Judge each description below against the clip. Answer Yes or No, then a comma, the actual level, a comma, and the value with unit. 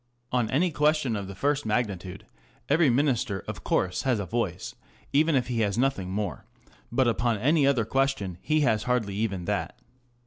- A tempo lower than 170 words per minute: No, average, 175 wpm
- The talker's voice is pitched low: Yes, low, 120 Hz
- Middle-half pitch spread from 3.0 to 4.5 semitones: No, wide, 5.4 semitones